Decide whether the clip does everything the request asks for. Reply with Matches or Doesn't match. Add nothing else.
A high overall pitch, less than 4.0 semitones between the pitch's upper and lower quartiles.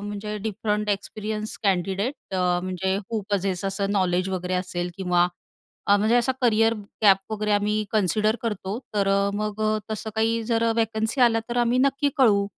Matches